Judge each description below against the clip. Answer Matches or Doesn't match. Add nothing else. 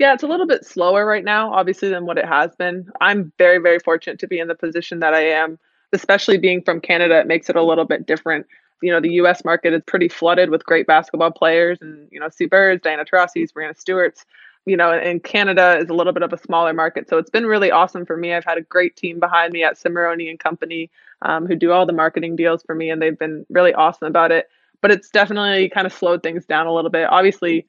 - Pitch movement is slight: Matches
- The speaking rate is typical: Doesn't match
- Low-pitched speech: Doesn't match